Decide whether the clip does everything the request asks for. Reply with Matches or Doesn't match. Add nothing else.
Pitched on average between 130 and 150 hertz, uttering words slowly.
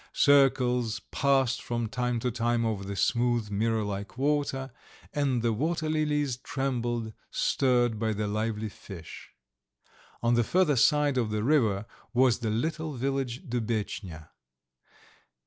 Doesn't match